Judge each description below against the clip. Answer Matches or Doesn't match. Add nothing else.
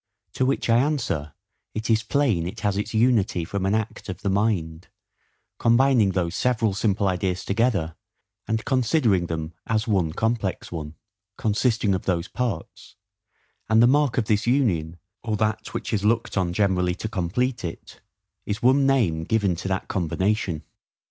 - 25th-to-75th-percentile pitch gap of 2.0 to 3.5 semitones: Doesn't match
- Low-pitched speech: Matches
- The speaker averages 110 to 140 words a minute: Doesn't match